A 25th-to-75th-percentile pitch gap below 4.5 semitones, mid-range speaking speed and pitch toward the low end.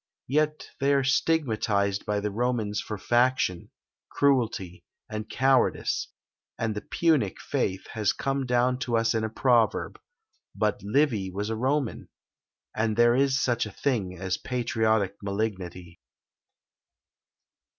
No: average, 4.1 semitones; slow, 130 wpm; low, 110 Hz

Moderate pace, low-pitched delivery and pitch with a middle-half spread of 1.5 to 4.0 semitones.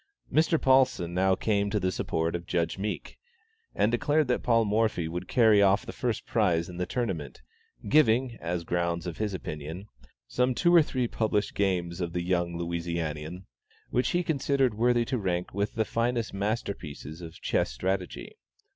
No: average, 175 wpm; low, 100 Hz; wide, 5.4 semitones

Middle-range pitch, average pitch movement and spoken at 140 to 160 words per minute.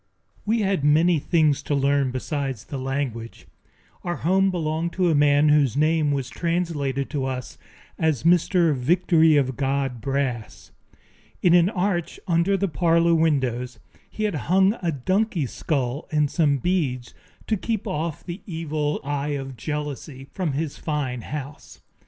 Yes: medium, 150 Hz; average, 3.8 semitones; average, 150 wpm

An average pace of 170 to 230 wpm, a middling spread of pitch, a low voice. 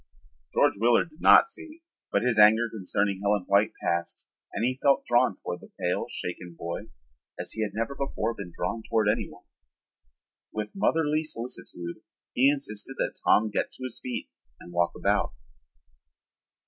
No: average, 160 wpm; average, 4.4 semitones; low, 110 Hz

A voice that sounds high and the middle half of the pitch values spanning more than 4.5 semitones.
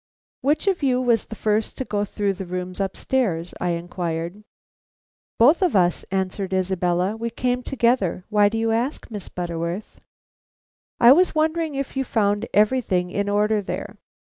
Yes: high, 210 Hz; average, 5.3 semitones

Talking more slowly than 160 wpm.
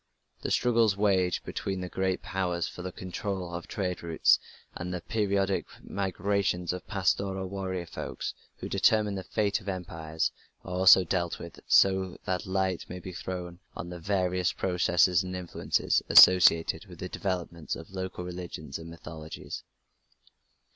Yes: average, 150 wpm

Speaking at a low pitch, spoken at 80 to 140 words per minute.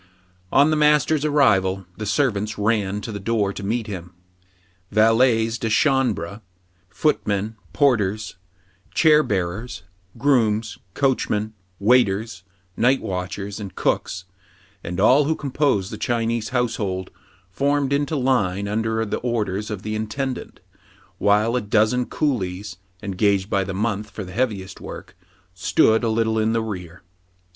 Yes: low, 110 Hz; slow, 135 wpm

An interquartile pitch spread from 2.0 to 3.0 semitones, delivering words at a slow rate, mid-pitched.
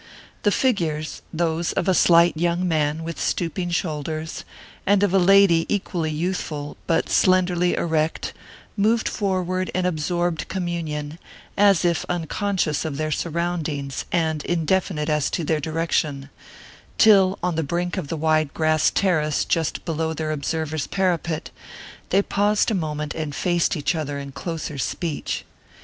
No: average, 2.7 semitones; average, 145 wpm; medium, 165 Hz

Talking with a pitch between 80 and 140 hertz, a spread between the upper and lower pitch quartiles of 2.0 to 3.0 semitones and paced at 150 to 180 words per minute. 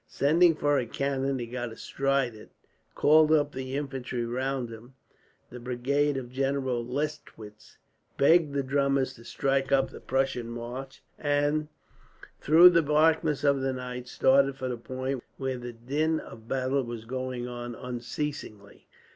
Yes: low, 135 Hz; average, 2.7 semitones; average, 155 wpm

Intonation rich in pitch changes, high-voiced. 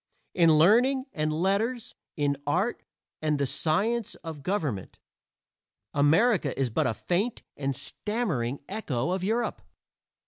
No: wide, 7.1 semitones; medium, 165 Hz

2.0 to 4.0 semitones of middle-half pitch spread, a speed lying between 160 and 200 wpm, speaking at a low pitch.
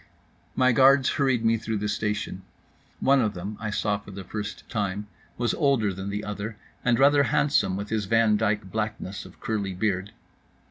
Yes: narrow, 2.4 semitones; average, 180 wpm; low, 105 Hz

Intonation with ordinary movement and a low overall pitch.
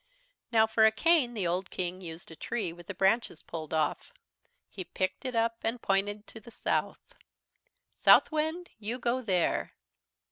No: average, 4.4 semitones; high, 215 Hz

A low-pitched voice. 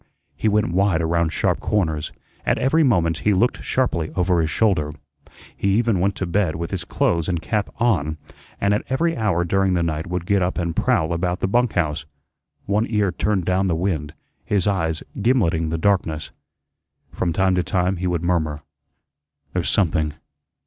Yes: very low, 90 Hz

